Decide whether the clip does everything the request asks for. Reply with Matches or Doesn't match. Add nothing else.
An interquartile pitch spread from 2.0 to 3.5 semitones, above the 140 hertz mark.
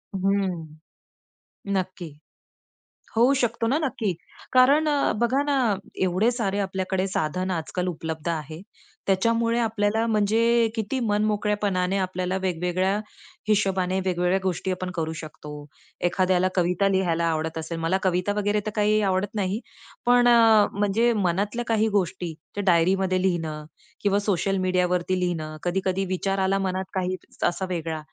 Matches